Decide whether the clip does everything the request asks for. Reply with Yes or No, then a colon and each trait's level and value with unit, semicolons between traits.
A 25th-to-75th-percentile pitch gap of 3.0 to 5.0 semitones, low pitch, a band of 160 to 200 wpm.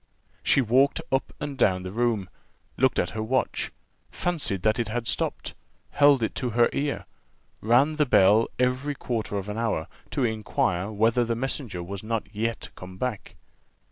Yes: average, 3.9 semitones; low, 115 Hz; average, 170 wpm